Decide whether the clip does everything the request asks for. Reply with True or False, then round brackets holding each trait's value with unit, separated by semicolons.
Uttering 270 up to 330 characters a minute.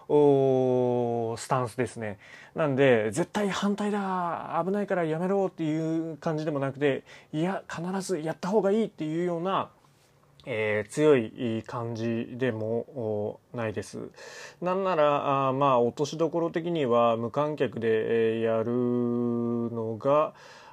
False (255 characters per minute)